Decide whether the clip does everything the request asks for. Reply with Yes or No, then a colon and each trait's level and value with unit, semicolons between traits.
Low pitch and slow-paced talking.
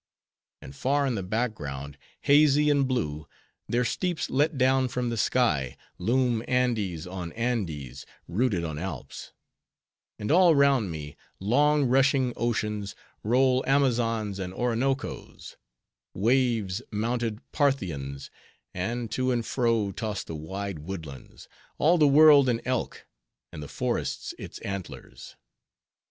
Yes: low, 115 Hz; slow, 125 wpm